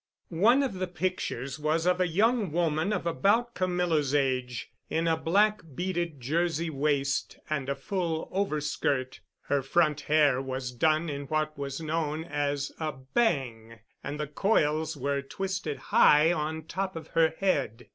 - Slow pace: No, average, 155 wpm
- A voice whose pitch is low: No, medium, 155 Hz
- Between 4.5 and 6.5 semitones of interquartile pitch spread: No, average, 3.9 semitones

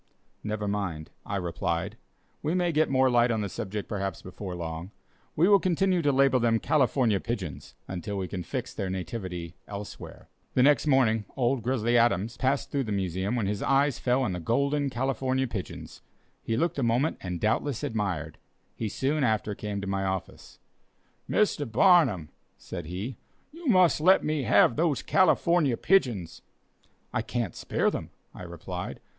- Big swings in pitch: Yes, wide, 6.1 semitones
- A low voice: Yes, low, 115 Hz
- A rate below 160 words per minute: No, average, 165 wpm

